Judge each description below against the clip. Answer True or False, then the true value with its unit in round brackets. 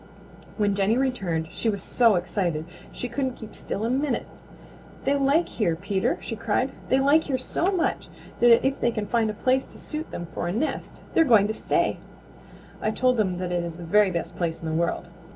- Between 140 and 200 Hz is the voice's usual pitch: False (220 Hz)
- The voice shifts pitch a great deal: True (6.3 semitones)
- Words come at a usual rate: False (210 wpm)